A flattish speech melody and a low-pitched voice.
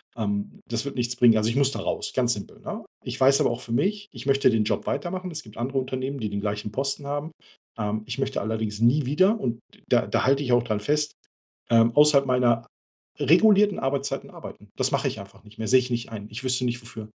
No: average, 3.8 semitones; low, 125 Hz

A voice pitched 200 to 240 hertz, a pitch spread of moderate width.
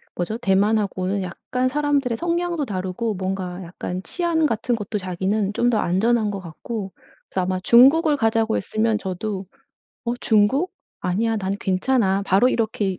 Yes: high, 215 Hz; average, 4.2 semitones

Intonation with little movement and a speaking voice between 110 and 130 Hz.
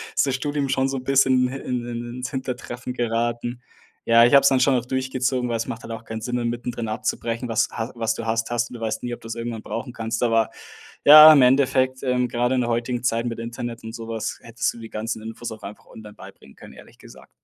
Yes: narrow, 1.9 semitones; low, 120 Hz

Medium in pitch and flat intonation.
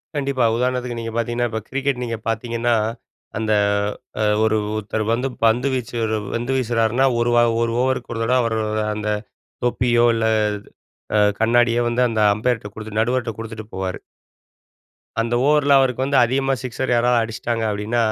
No: low, 120 Hz; narrow, 2.0 semitones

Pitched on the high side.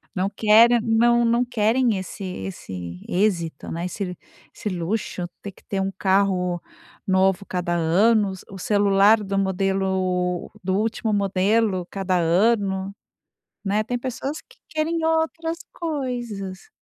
Yes: high, 195 Hz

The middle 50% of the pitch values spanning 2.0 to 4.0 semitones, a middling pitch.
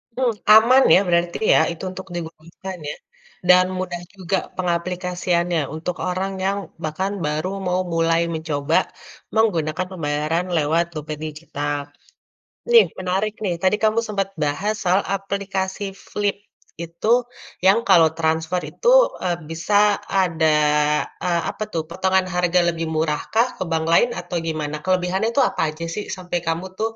Yes: average, 2.9 semitones; medium, 180 Hz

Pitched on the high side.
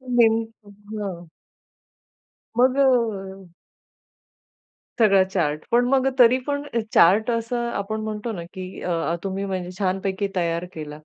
Yes: high, 200 Hz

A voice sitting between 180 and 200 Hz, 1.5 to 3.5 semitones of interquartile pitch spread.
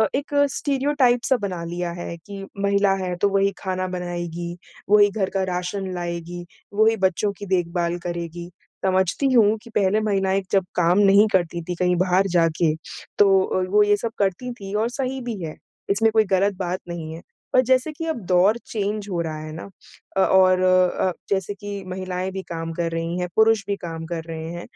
Yes: high, 190 Hz; average, 2.9 semitones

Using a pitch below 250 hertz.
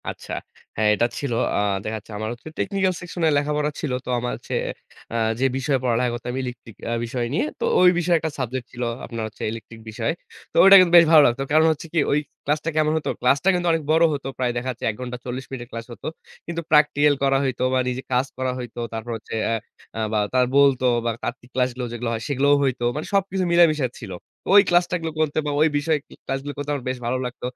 Yes: low, 135 Hz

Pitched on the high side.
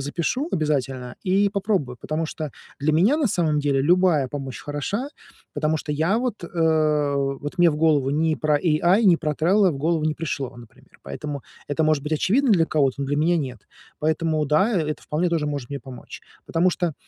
No: medium, 155 Hz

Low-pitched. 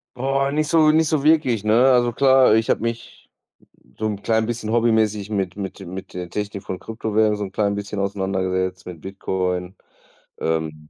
Yes: low, 105 Hz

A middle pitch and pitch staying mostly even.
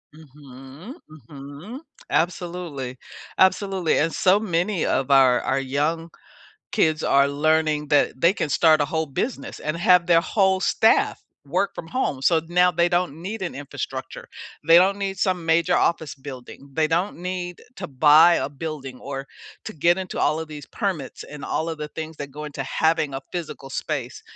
No: medium, 160 Hz; average, 3.9 semitones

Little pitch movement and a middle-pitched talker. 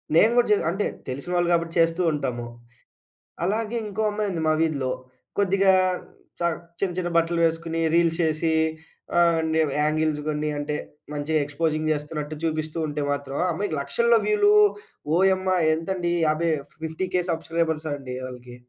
No: average, 3.2 semitones; medium, 165 Hz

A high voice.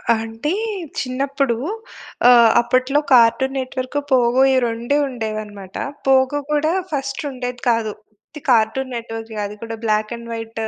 Yes: high, 240 Hz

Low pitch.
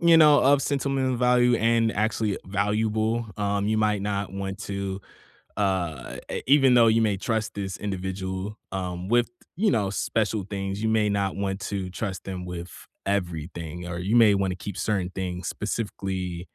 Yes: low, 100 Hz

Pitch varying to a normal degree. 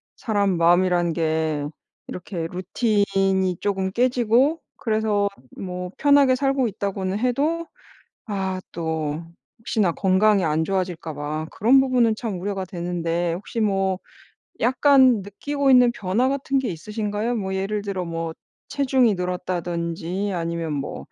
Yes: average, 5.0 semitones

